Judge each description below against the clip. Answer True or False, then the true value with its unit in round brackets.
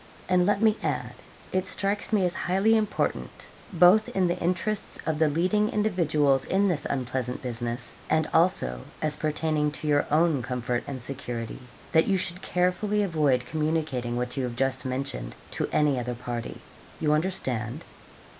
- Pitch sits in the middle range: True (155 Hz)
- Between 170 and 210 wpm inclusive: False (160 wpm)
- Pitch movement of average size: False (6.4 semitones)